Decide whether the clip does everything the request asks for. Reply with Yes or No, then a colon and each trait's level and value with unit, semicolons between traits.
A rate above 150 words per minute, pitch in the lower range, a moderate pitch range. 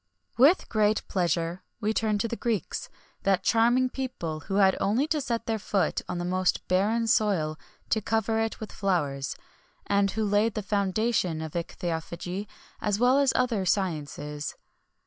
No: average, 165 wpm; high, 205 Hz; average, 4.2 semitones